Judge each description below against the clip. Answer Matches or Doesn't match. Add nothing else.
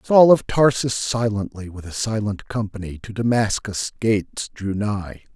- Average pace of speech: Matches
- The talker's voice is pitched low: Matches